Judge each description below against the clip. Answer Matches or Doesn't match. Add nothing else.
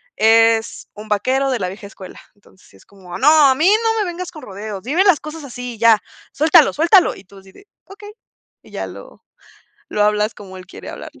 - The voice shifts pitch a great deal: Matches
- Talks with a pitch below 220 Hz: Doesn't match